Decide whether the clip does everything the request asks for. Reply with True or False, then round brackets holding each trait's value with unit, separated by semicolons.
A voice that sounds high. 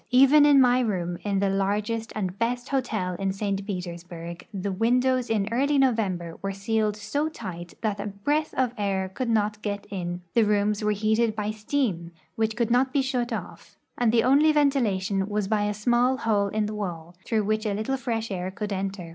True (210 Hz)